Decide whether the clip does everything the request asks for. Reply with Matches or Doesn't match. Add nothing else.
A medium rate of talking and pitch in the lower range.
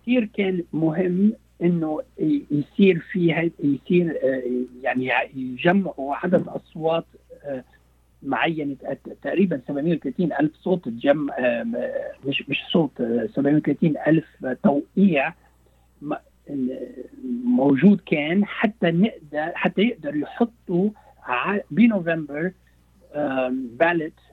Doesn't match